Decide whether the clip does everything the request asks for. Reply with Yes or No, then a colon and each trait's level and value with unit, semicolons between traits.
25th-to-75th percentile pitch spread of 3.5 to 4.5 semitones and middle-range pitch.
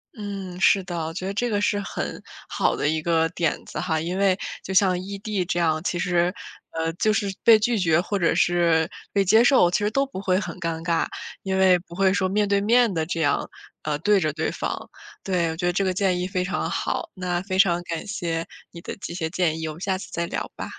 No: average, 2.9 semitones; medium, 180 Hz